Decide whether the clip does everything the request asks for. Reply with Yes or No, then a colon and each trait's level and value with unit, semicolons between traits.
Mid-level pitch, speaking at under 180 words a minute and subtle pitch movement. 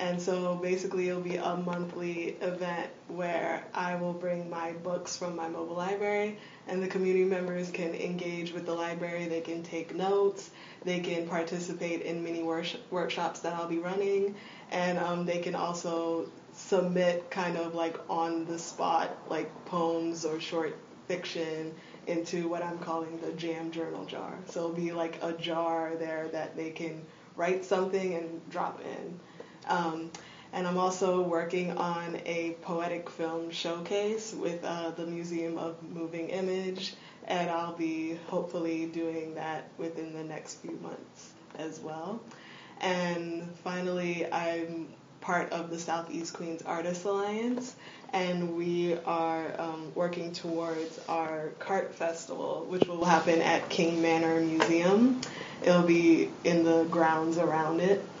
Yes: medium, 170 Hz; average, 150 wpm; narrow, 1.4 semitones